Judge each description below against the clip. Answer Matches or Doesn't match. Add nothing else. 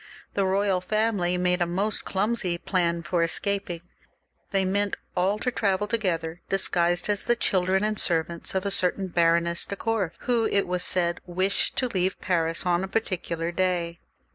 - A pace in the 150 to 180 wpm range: Matches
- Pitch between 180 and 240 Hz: Matches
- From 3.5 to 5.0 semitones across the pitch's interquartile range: Doesn't match